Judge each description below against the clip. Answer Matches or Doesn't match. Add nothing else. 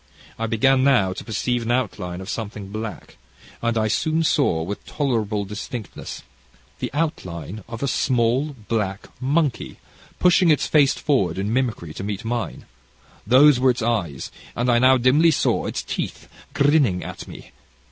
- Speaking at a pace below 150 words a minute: Doesn't match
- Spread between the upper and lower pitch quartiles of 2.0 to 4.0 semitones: Doesn't match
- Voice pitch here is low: Matches